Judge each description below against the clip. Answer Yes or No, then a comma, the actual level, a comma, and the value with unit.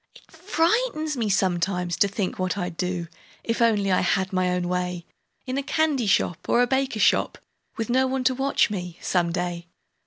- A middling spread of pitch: No, wide, 6.6 semitones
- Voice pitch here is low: No, high, 195 Hz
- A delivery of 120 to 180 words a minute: No, average, 190 wpm